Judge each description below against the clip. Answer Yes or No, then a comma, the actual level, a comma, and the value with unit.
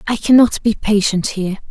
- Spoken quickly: No, average, 175 wpm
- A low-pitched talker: No, high, 210 Hz